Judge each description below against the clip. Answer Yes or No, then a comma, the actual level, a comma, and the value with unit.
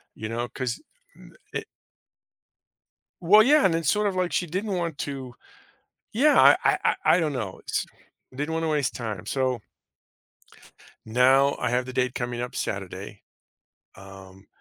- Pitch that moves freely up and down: Yes, wide, 6.1 semitones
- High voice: No, low, 130 Hz